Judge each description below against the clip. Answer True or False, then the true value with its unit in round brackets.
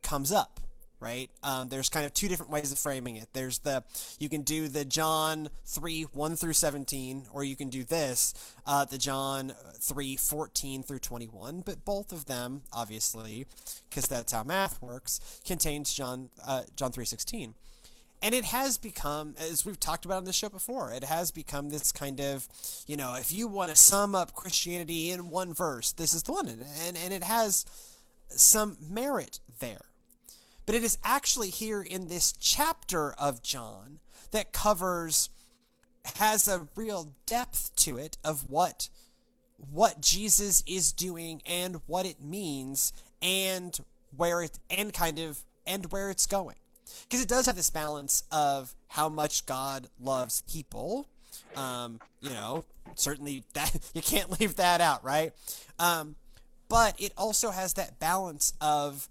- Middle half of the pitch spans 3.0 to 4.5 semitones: False (5.6 semitones)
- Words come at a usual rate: True (165 wpm)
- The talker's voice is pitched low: False (155 Hz)